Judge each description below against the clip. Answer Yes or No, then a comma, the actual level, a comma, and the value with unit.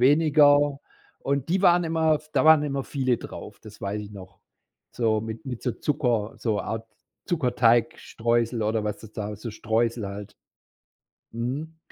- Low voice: Yes, low, 120 Hz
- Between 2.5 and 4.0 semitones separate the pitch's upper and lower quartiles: No, average, 4.9 semitones